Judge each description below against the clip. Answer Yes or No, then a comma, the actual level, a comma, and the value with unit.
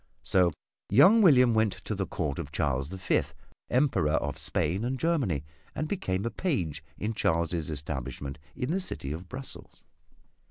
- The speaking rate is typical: Yes, average, 160 wpm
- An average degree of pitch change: No, wide, 9.0 semitones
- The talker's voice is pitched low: Yes, very low, 95 Hz